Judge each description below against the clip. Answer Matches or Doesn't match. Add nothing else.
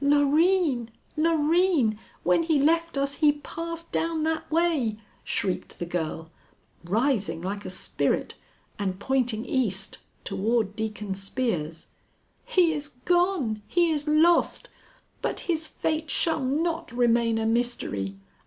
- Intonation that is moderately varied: Doesn't match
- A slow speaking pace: Matches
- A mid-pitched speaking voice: Doesn't match